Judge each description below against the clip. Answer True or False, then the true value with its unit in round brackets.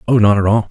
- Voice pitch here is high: False (105 Hz)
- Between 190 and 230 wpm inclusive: False (255 wpm)